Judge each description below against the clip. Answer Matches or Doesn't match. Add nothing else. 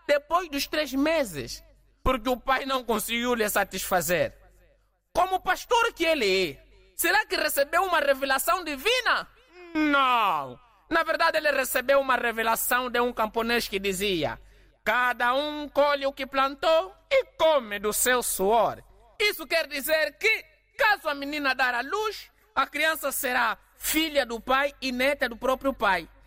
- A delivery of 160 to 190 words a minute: Doesn't match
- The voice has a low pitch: Doesn't match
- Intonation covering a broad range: Doesn't match